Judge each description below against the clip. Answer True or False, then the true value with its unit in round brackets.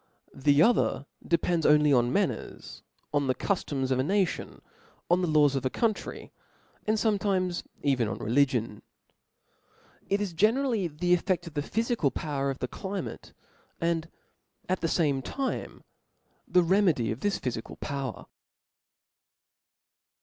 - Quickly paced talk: False (140 wpm)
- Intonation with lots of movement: True (5.8 semitones)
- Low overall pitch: False (160 Hz)